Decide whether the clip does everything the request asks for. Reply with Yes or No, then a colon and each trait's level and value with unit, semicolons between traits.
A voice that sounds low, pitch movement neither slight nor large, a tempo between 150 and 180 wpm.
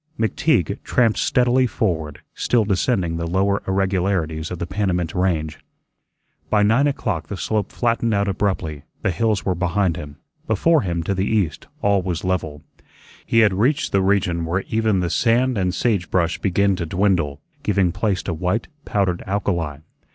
Yes: very low, 95 Hz; average, 3.6 semitones; average, 165 wpm